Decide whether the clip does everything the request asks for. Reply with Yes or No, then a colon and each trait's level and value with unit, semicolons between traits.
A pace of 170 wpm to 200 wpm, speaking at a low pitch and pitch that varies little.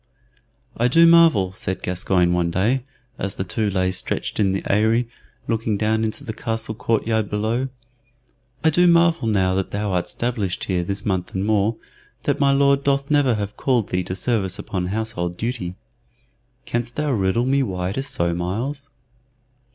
No: average, 175 wpm; low, 110 Hz; average, 5.0 semitones